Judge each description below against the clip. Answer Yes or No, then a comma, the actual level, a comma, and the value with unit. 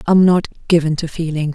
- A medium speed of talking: Yes, average, 195 wpm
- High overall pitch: No, medium, 165 Hz